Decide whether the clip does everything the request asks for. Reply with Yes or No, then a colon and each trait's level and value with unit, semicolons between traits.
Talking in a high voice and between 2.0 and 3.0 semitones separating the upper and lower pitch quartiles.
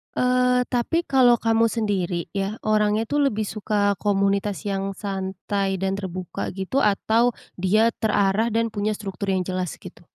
Yes: high, 205 Hz; average, 2.7 semitones